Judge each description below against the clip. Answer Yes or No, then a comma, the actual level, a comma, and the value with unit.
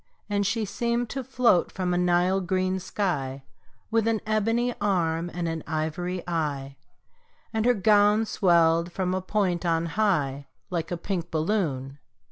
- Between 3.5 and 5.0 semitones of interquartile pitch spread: Yes, average, 4.2 semitones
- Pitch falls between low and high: Yes, medium, 180 Hz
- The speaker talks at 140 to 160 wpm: Yes, average, 150 wpm